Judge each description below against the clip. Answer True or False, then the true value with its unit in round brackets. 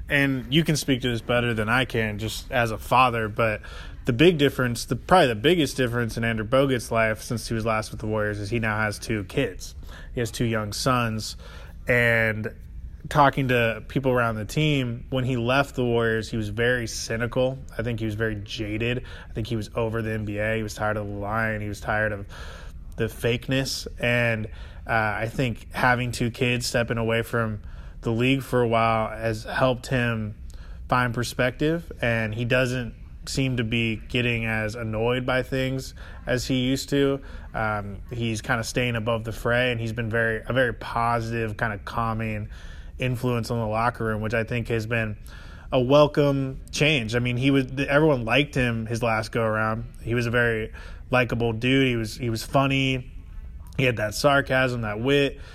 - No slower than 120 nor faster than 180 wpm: False (195 wpm)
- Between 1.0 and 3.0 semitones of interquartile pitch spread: True (2.7 semitones)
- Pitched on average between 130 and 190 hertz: False (115 Hz)